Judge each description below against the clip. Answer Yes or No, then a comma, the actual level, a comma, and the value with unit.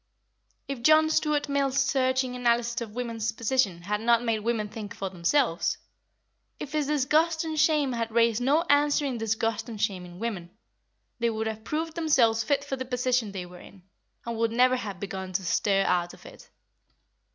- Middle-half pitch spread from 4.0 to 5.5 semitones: Yes, average, 4.6 semitones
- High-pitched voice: Yes, high, 235 Hz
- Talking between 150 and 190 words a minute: Yes, average, 180 wpm